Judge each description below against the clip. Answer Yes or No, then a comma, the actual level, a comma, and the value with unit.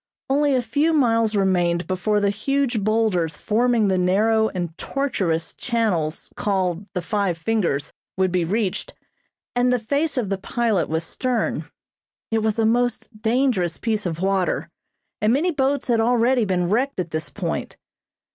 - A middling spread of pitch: Yes, average, 4.9 semitones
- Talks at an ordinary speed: Yes, average, 155 wpm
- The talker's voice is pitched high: Yes, high, 215 Hz